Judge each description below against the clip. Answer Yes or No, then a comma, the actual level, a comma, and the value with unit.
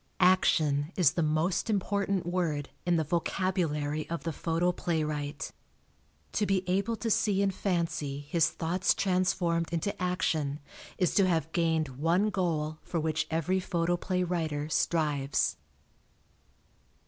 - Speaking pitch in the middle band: Yes, medium, 170 Hz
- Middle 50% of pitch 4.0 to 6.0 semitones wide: No, average, 3.1 semitones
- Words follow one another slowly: Yes, slow, 125 wpm